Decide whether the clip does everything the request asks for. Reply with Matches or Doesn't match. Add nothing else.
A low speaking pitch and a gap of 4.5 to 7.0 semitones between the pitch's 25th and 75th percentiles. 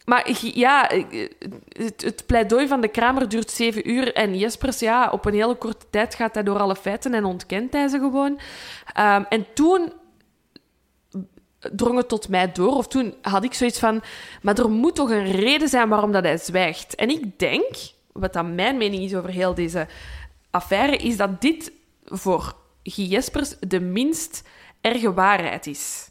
Doesn't match